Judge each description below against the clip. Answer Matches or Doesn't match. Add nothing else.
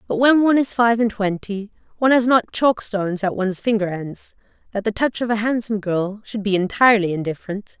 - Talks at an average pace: Doesn't match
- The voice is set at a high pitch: Matches